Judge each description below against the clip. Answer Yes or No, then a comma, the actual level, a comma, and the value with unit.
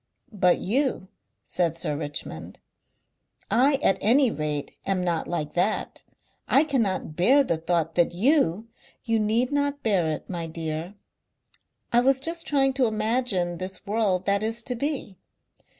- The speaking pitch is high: Yes, high, 205 Hz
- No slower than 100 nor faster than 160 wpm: Yes, average, 150 wpm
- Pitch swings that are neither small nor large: No, wide, 6.7 semitones